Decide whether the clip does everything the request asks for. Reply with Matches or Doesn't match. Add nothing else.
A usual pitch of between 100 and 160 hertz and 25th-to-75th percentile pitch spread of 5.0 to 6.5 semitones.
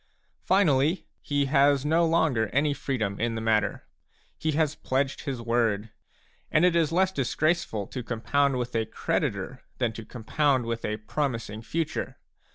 Matches